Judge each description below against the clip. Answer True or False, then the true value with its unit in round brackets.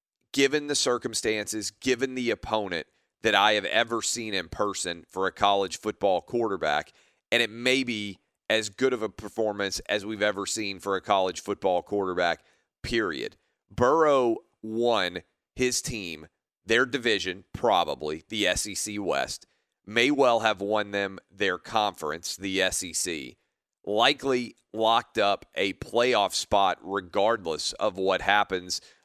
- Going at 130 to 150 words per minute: True (135 wpm)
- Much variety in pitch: False (3.3 semitones)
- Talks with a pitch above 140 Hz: False (105 Hz)